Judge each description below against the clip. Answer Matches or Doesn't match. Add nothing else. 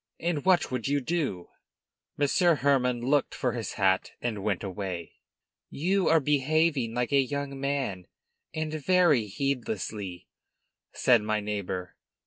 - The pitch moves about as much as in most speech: Doesn't match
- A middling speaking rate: Doesn't match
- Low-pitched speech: Matches